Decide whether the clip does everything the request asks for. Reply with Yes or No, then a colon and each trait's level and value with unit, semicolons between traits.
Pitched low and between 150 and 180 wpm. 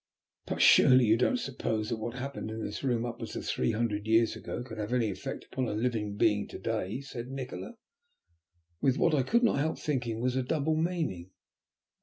No: low, 120 Hz; average, 200 wpm